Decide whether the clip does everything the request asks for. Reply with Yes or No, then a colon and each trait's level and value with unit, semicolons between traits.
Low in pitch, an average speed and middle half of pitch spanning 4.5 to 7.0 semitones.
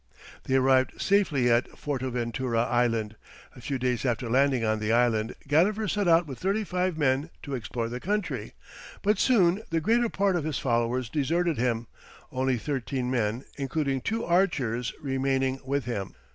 Yes: low, 130 Hz; average, 160 wpm; wide, 5.5 semitones